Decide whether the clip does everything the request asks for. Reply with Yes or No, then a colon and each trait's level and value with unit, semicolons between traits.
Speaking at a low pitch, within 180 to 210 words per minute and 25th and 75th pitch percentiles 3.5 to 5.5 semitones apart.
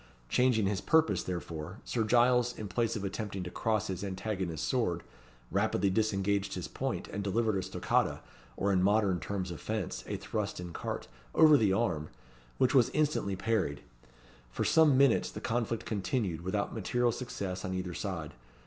No: low, 100 Hz; average, 165 wpm; average, 4.0 semitones